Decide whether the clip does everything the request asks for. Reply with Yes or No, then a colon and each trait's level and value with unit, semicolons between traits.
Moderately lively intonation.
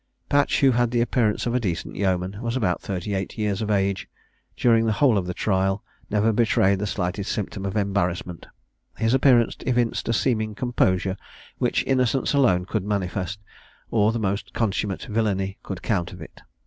Yes: average, 3.4 semitones